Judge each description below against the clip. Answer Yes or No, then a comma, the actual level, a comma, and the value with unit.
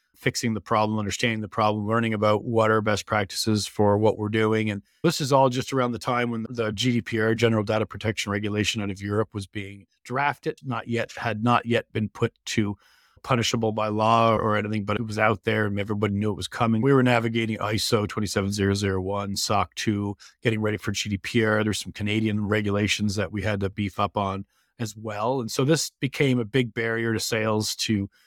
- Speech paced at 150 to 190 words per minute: No, average, 200 wpm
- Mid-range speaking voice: No, low, 110 Hz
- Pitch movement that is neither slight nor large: No, narrow, 1.9 semitones